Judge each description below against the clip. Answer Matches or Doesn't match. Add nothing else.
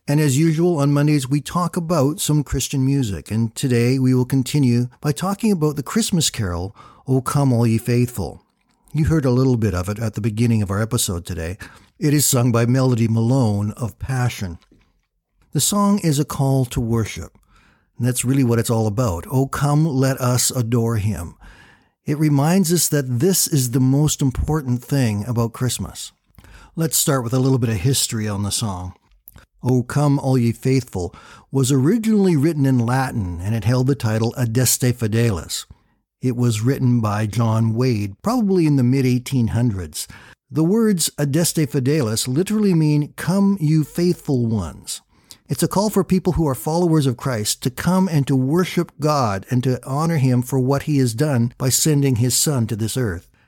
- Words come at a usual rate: Matches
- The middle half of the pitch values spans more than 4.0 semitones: Matches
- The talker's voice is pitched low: Matches